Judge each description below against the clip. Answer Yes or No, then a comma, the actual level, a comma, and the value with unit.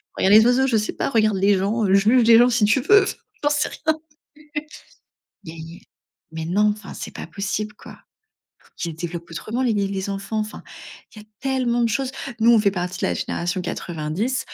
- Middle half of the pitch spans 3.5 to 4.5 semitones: Yes, average, 4.1 semitones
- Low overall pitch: No, high, 210 Hz